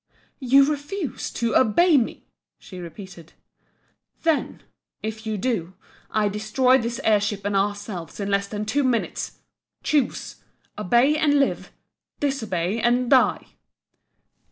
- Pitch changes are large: No, average, 4.8 semitones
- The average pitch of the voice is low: No, high, 225 Hz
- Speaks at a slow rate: Yes, slow, 125 wpm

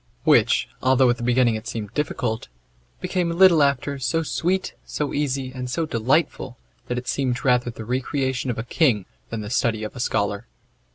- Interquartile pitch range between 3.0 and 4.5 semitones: Yes, average, 3.4 semitones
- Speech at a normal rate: Yes, average, 185 wpm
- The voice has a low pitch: Yes, low, 125 Hz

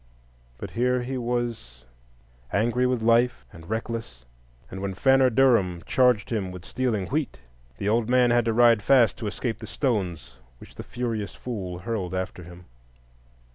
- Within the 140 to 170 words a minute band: Yes, average, 160 wpm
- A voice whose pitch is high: No, low, 115 Hz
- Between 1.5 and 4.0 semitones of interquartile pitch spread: No, average, 4.8 semitones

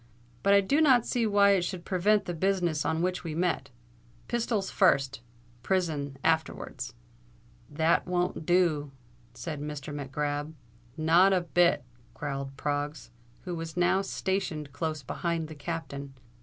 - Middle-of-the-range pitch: Yes, medium, 165 Hz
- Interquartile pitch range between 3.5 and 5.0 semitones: Yes, average, 4.1 semitones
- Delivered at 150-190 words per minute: No, average, 140 wpm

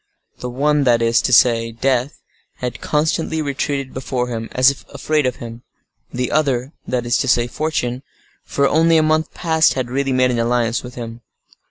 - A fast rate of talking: No, average, 165 wpm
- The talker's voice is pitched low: Yes, low, 130 Hz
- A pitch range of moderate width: Yes, average, 3.3 semitones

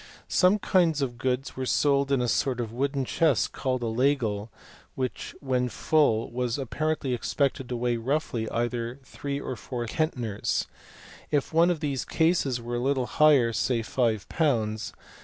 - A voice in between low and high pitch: No, low, 130 Hz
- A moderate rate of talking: Yes, average, 160 wpm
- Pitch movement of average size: Yes, average, 3.2 semitones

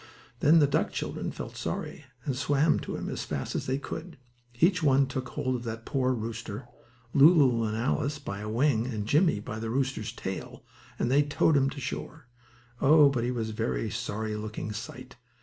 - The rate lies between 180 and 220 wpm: Yes, average, 190 wpm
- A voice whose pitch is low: Yes, low, 130 Hz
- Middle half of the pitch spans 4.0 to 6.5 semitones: Yes, average, 4.4 semitones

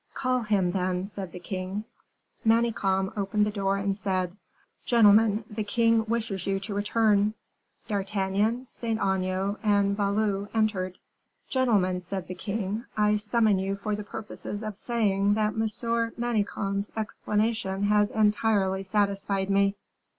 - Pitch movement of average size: No, narrow, 2.0 semitones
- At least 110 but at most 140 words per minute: Yes, slow, 135 wpm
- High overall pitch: Yes, high, 205 Hz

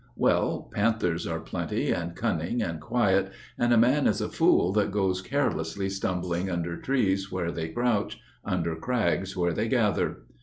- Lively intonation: No, average, 4.0 semitones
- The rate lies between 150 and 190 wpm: Yes, average, 160 wpm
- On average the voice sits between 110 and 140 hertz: No, very low, 95 Hz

